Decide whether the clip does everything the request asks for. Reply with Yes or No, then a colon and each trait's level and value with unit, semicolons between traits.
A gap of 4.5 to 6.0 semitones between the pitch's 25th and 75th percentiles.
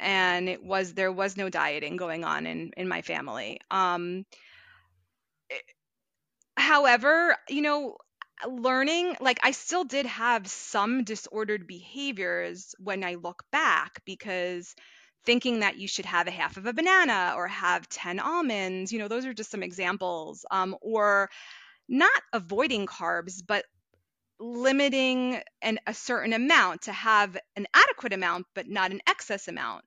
Yes: wide, 5.6 semitones